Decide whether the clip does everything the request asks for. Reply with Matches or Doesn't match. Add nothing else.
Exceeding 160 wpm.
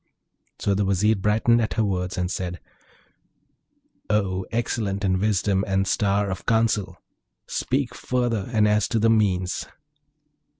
Doesn't match